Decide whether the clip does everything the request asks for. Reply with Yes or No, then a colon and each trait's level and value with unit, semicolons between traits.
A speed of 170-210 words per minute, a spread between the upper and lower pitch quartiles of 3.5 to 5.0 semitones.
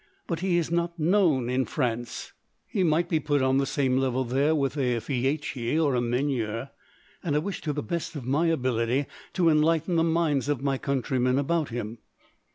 Yes: average, 190 wpm; average, 4.2 semitones